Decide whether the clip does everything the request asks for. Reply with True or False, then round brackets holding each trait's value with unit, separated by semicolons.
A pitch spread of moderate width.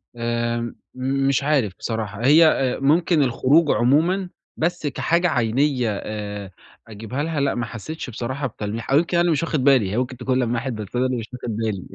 True (4.2 semitones)